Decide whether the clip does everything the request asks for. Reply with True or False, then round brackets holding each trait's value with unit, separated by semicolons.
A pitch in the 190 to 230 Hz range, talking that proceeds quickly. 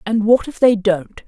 True (215 Hz; 235 wpm)